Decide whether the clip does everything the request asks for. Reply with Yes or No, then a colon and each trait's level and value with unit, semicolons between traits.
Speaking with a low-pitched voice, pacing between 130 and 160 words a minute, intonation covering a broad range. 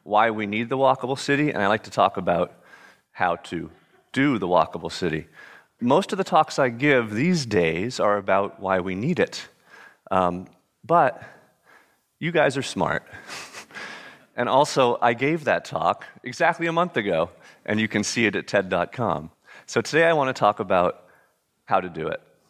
No: low, 120 Hz; average, 175 wpm; wide, 7.2 semitones